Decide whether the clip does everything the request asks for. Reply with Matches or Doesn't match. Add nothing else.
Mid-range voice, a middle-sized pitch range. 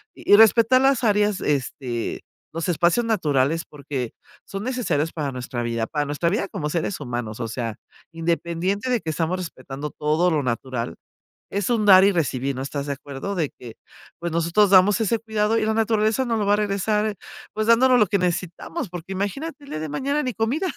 Doesn't match